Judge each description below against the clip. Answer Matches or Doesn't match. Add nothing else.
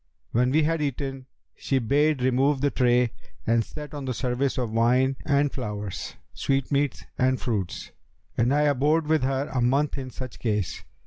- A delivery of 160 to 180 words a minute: Matches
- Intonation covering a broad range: Doesn't match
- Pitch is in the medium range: Doesn't match